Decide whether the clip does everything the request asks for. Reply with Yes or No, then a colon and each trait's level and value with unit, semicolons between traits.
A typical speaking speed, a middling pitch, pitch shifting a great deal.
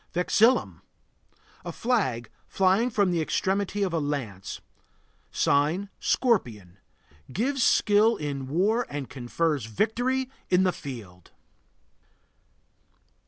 No: slow, 100 wpm; medium, 180 Hz; wide, 8.1 semitones